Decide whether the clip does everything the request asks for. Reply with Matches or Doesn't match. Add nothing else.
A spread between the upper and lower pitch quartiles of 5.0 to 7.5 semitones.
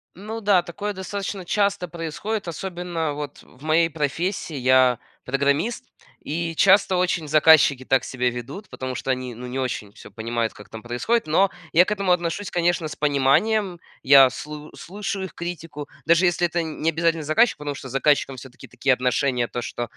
Matches